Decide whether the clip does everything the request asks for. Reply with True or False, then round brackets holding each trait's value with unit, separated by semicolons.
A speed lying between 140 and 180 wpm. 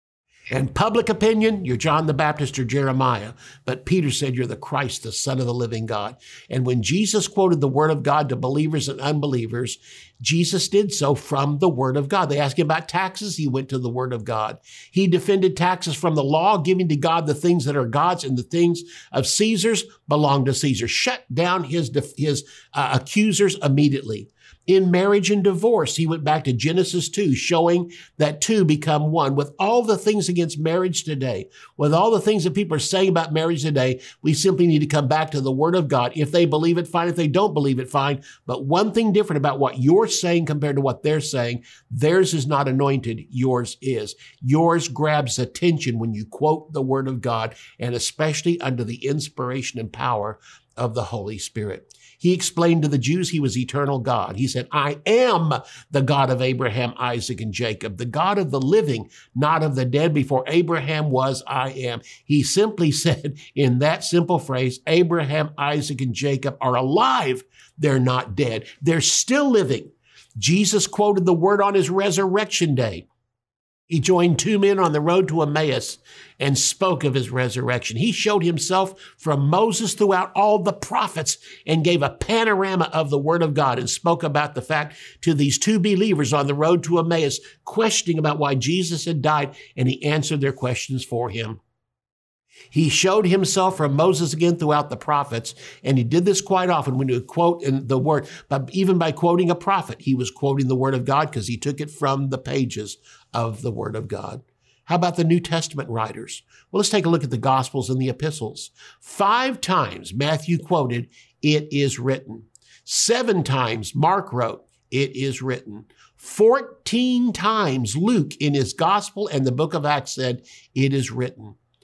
False (190 wpm)